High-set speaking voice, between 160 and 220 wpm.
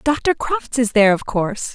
Yes: high, 245 Hz; fast, 205 wpm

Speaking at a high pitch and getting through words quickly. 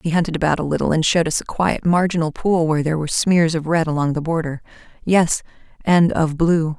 No: medium, 160 Hz; fast, 220 wpm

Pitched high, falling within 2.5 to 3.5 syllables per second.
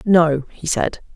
No: medium, 165 Hz; 3.3 syllables/s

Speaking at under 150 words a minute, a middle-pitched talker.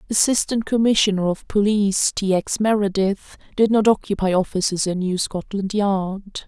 No: average, 140 wpm; high, 200 Hz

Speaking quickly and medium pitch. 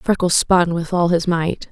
Yes: fast, 210 wpm; medium, 175 Hz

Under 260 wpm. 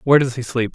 No: fast, 325 wpm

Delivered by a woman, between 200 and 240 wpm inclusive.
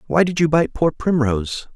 No: male; fast, 205 wpm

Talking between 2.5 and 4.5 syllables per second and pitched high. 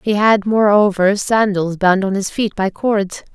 Yes: 4.1 syllables/s; high, 200 Hz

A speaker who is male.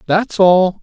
Yes: male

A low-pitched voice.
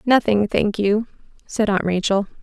No: high, 210 Hz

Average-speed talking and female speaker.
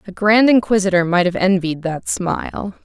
Yes: average, 170 wpm; female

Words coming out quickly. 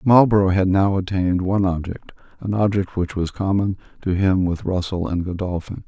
No: average, 175 wpm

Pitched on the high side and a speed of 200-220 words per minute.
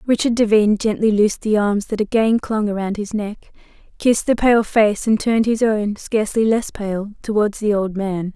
No: high, 215 Hz; average, 180 wpm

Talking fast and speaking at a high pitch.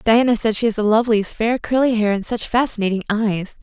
Yes: fast, 215 wpm; high, 220 Hz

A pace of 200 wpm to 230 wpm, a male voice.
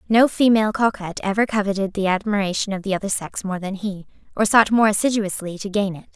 No: fast, 205 wpm; female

